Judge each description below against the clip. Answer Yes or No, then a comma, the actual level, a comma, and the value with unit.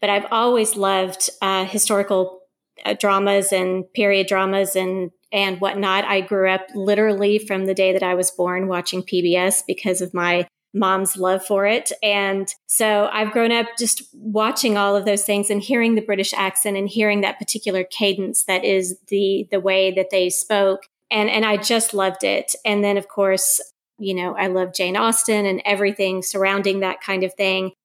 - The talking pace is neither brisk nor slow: Yes, average, 185 wpm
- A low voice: No, high, 195 Hz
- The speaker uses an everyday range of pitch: No, narrow, 1.7 semitones